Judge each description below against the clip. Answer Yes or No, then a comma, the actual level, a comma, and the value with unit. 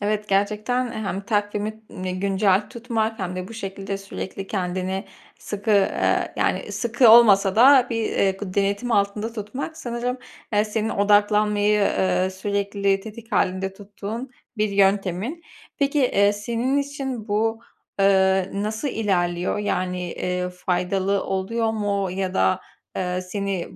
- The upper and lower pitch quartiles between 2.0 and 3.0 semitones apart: Yes, narrow, 2.6 semitones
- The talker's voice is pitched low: No, high, 205 Hz